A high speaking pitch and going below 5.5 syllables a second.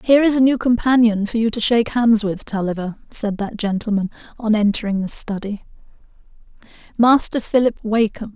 No: high, 220 Hz; 5.6 syllables/s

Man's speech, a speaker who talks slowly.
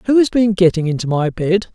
No: male; fast, 240 wpm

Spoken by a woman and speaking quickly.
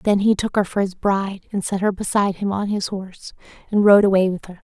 Yes: female; fast, 255 wpm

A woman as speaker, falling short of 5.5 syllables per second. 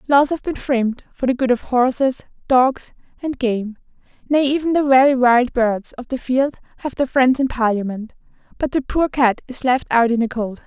Yes: female; 4.9 syllables/s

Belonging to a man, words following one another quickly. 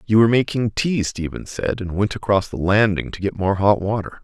Yes: male; fast, 225 wpm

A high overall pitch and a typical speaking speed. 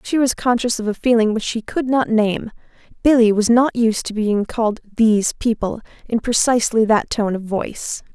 Yes: high, 225 Hz; average, 190 wpm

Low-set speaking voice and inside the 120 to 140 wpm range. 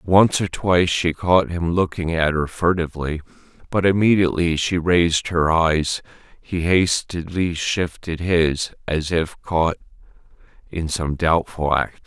Yes: very low, 85 Hz; slow, 135 wpm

